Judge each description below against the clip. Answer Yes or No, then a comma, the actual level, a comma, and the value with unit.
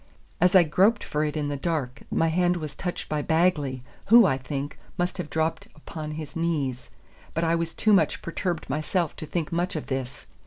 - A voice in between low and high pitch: Yes, medium, 160 Hz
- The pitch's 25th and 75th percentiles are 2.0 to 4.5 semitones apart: Yes, average, 3.1 semitones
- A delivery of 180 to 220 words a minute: Yes, average, 200 wpm